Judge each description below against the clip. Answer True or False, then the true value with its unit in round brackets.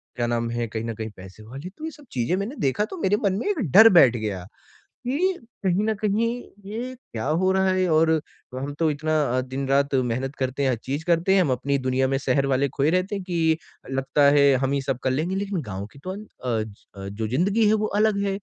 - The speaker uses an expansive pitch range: True (6.8 semitones)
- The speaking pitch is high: False (140 Hz)